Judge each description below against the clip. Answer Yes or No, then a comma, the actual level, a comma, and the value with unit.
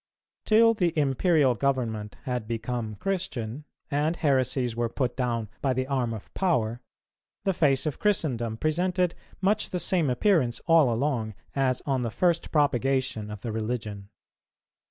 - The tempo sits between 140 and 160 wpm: Yes, average, 145 wpm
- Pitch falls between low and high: No, low, 130 Hz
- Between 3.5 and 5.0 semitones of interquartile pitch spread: No, wide, 5.6 semitones